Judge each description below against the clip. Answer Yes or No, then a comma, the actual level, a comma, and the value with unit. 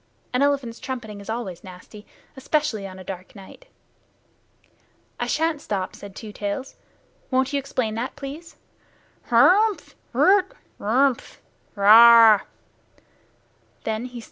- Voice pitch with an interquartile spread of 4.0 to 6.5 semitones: Yes, wide, 5.4 semitones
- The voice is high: Yes, high, 235 Hz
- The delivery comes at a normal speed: No, slow, 110 wpm